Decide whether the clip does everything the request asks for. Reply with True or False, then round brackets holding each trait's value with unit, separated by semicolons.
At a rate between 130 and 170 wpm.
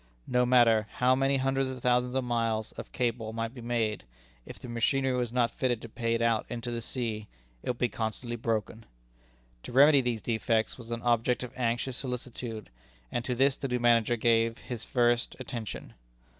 False (190 wpm)